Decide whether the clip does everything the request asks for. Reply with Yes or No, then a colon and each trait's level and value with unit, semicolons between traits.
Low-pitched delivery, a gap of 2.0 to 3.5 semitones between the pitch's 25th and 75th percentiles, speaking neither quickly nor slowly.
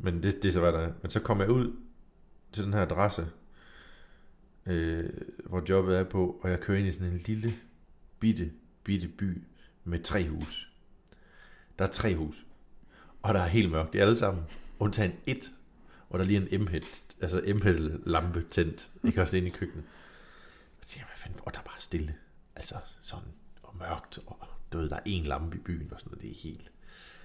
Yes: very low, 90 Hz; average, 3.2 semitones; average, 205 wpm